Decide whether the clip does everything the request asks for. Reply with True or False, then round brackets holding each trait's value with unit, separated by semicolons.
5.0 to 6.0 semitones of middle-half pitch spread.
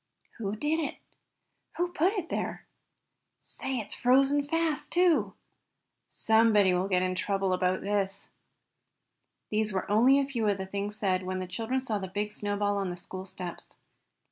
True (5.6 semitones)